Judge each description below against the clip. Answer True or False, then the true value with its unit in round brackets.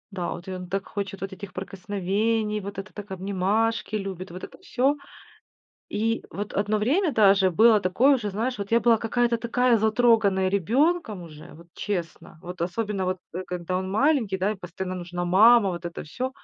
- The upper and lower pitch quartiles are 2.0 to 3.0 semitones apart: False (3.5 semitones)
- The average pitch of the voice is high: True (200 Hz)